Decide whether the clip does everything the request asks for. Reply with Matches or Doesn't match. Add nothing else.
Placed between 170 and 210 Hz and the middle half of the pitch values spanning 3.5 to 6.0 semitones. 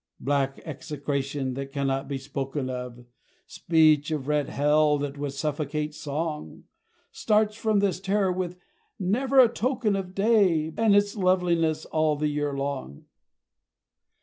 Doesn't match